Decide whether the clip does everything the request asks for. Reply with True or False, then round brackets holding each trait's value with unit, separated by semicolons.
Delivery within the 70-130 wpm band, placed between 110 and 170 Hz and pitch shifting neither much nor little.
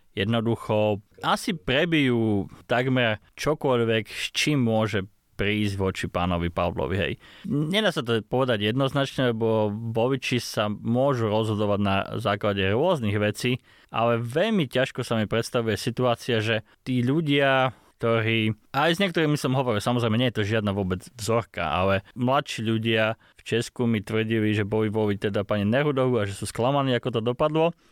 False (145 wpm; 115 Hz; 3.4 semitones)